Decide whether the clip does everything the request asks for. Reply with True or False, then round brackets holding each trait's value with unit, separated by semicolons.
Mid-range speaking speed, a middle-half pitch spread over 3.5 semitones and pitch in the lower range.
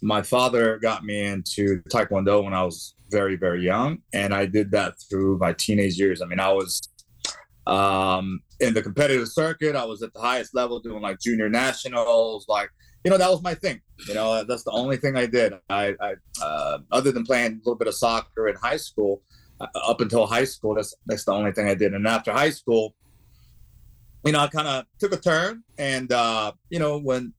False (215 wpm; 4.9 semitones; 110 Hz)